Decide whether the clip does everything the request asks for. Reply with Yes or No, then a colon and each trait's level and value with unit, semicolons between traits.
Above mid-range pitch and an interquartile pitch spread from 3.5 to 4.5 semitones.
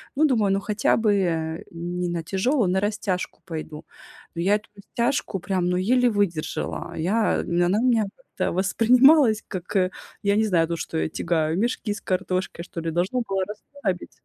Yes: high, 195 Hz; average, 3.8 semitones